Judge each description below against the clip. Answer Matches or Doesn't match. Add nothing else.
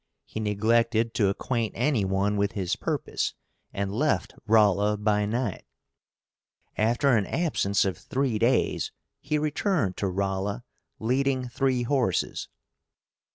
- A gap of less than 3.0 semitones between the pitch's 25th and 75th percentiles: Doesn't match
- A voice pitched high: Doesn't match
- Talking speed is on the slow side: Matches